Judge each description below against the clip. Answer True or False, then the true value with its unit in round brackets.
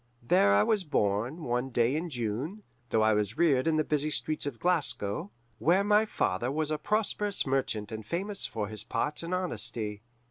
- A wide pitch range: True (7.5 semitones)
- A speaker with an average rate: True (185 wpm)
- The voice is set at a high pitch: False (135 Hz)